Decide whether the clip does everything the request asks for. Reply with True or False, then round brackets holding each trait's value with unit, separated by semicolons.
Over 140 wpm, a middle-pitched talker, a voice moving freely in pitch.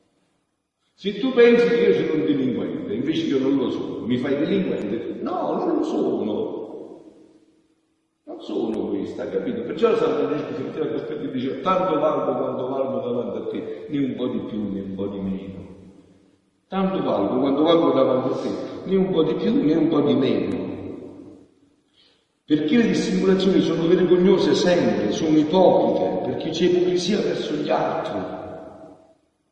True (165 wpm; 175 Hz; 7.3 semitones)